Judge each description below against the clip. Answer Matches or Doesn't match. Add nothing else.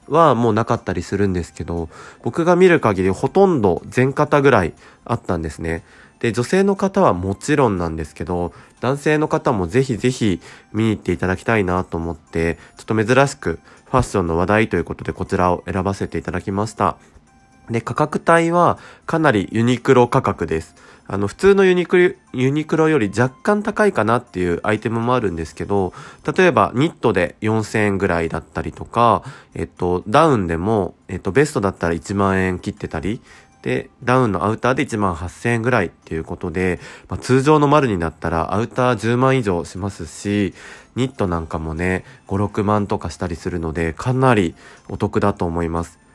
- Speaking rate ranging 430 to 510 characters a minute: Doesn't match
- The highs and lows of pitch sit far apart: Matches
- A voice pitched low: Matches